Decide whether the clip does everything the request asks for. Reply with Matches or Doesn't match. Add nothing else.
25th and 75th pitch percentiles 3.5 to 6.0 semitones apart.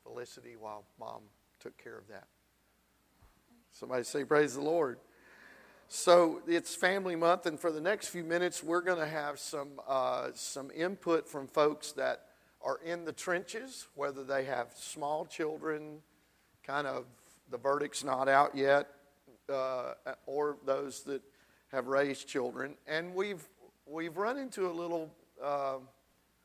Matches